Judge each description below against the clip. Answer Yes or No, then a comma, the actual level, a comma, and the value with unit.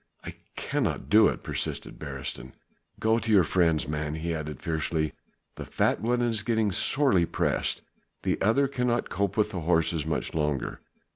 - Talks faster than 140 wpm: Yes, average, 160 wpm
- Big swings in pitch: Yes, wide, 6.1 semitones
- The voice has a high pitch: No, very low, 90 Hz